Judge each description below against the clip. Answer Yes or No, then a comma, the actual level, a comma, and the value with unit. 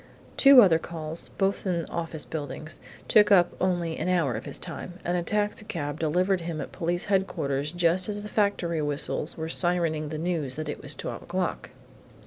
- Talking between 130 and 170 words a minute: No, average, 180 wpm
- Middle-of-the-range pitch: Yes, medium, 170 Hz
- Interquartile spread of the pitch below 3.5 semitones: Yes, average, 3.1 semitones